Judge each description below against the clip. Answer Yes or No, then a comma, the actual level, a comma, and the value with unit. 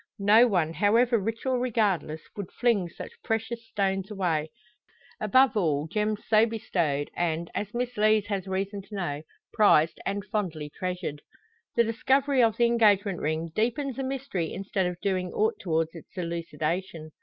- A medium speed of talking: Yes, average, 155 wpm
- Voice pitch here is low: No, high, 200 Hz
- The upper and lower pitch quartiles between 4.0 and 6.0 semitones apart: Yes, average, 4.8 semitones